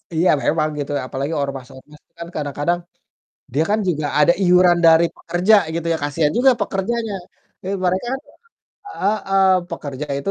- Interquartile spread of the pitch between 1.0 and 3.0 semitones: No, average, 4.6 semitones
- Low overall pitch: No, medium, 170 Hz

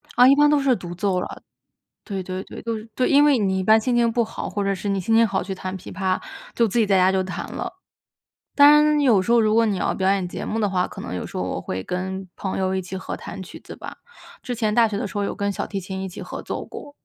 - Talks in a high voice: Yes, high, 200 Hz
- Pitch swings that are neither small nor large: Yes, average, 3.5 semitones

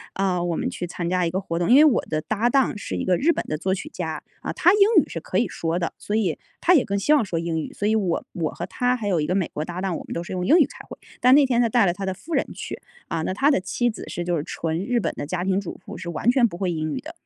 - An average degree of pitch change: No, wide, 6.0 semitones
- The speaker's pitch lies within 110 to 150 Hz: No, high, 190 Hz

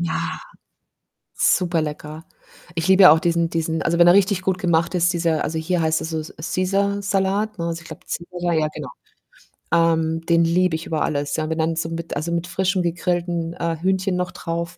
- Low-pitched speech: No, medium, 170 Hz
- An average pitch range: No, narrow, 2.0 semitones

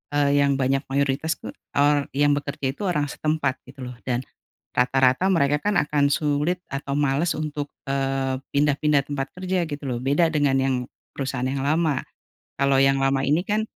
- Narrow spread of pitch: Yes, narrow, 1.8 semitones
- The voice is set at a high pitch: No, medium, 140 Hz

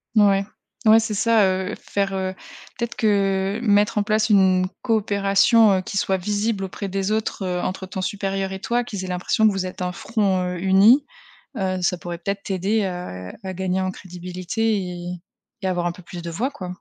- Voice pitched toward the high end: Yes, high, 195 Hz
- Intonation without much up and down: Yes, narrow, 2.2 semitones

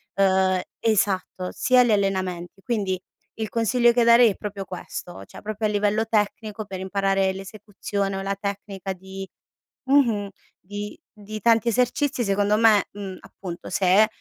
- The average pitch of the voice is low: No, high, 205 Hz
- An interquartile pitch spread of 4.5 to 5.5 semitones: No, narrow, 2.4 semitones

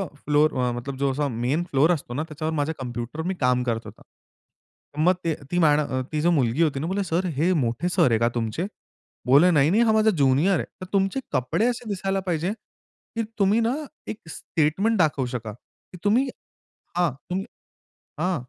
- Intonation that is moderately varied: No, wide, 5.9 semitones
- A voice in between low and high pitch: Yes, medium, 155 Hz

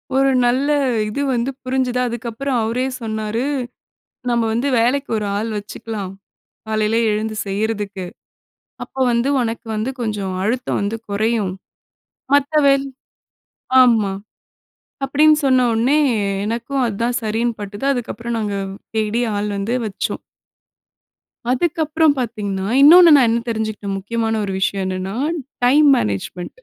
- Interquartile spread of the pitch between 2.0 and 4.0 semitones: Yes, average, 3.5 semitones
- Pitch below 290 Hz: Yes, high, 225 Hz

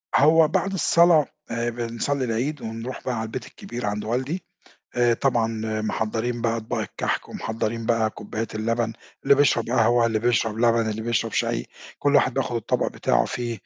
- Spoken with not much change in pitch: Yes, narrow, 2.3 semitones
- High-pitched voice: No, low, 115 Hz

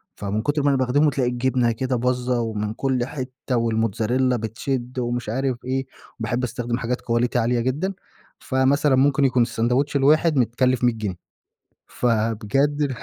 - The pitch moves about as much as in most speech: No, narrow, 2.3 semitones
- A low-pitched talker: Yes, low, 125 Hz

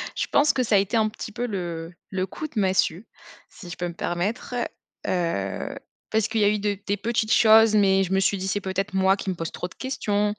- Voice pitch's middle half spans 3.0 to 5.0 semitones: No, narrow, 2.6 semitones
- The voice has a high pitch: Yes, high, 200 Hz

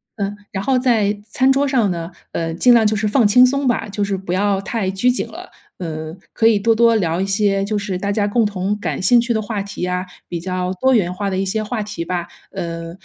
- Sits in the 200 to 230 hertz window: Yes, high, 205 Hz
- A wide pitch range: No, average, 3.6 semitones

